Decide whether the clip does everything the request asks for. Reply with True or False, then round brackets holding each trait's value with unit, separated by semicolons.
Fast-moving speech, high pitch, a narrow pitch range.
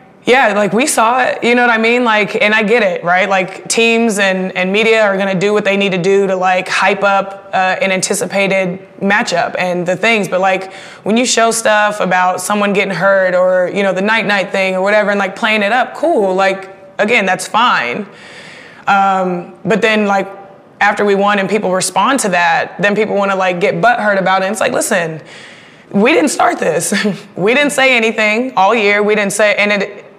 True (220 wpm; 200 Hz; 2.1 semitones)